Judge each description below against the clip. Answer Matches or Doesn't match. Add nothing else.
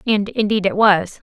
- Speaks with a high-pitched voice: Matches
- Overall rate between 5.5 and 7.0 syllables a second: Doesn't match